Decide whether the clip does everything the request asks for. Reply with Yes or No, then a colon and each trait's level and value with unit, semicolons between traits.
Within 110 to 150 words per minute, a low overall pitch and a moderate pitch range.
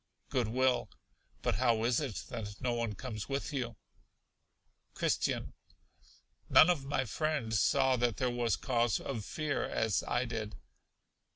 Yes: average, 145 wpm; low, 120 Hz; average, 3.0 semitones